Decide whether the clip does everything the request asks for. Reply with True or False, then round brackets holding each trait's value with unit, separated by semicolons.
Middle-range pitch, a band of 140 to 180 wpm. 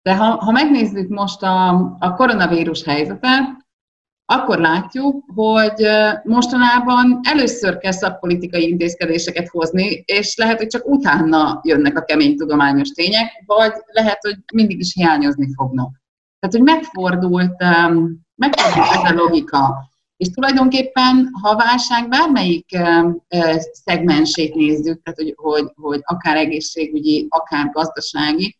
False (180 Hz; 120 wpm)